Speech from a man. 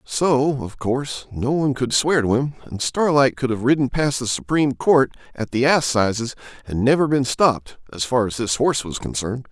Yes: male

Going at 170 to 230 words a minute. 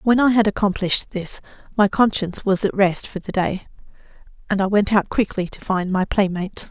Yes: average, 195 wpm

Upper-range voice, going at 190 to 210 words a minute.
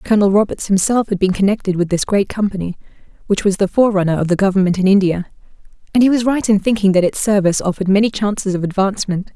Yes: high, 200 Hz; fast, 205 wpm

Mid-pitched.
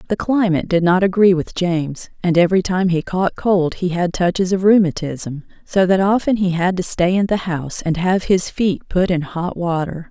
Yes: medium, 180 Hz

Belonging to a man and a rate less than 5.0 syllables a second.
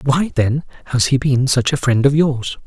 Yes: male; 4.6 syllables/s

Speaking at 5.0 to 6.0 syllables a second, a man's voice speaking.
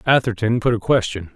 Yes: 5.7 syllables/s; male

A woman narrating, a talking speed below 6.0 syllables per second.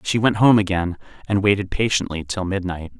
No: male; 5.5 syllables/s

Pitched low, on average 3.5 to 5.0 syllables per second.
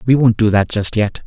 No: low, 110 Hz; 5.2 syllables/s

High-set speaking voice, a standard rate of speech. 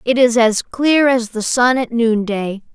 Yes: high, 235 Hz; average, 195 wpm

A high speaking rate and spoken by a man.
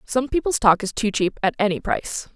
No: fast, 230 wpm; female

